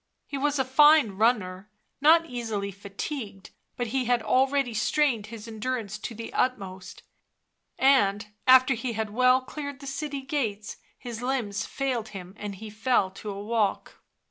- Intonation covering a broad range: No, average, 4.3 semitones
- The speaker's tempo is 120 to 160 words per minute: Yes, average, 155 wpm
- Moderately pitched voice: No, high, 235 Hz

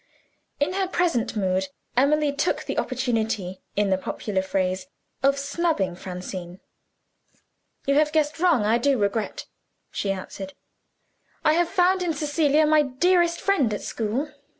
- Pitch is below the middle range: No, very high, 270 Hz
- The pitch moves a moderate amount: No, wide, 7.8 semitones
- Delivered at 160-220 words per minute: No, average, 140 wpm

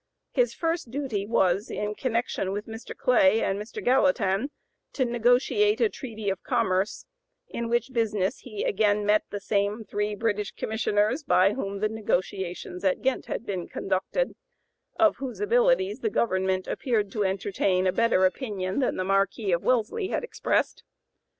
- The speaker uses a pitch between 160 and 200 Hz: No, high, 215 Hz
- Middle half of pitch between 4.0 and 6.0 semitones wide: Yes, average, 4.4 semitones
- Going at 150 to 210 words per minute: Yes, average, 155 wpm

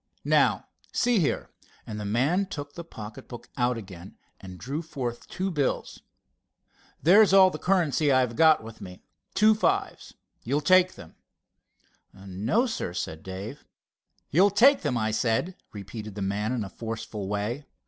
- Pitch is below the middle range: Yes, low, 125 Hz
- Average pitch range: No, wide, 8.7 semitones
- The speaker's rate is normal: Yes, average, 150 wpm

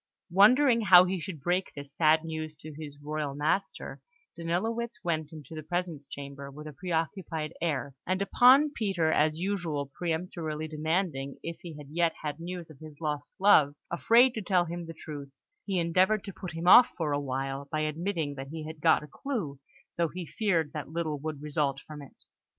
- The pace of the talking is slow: No, average, 185 wpm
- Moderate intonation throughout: Yes, average, 3.5 semitones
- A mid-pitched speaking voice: Yes, medium, 160 Hz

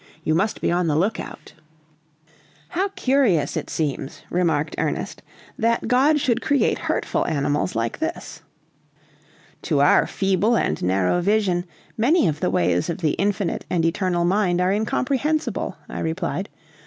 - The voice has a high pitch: No, medium, 180 Hz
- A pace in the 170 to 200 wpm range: No, average, 140 wpm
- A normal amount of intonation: No, wide, 6.0 semitones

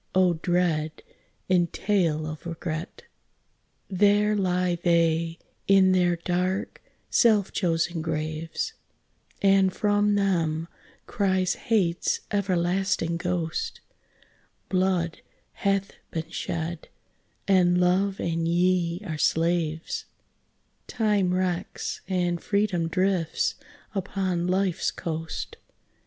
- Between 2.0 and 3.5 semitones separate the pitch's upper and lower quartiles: Yes, narrow, 2.5 semitones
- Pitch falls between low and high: Yes, medium, 180 Hz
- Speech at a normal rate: No, slow, 90 wpm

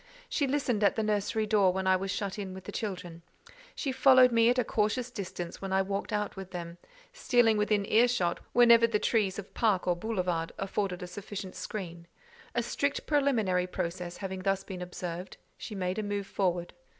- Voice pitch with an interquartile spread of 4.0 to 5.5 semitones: No, average, 3.5 semitones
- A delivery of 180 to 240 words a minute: Yes, average, 195 wpm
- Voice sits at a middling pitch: No, high, 200 Hz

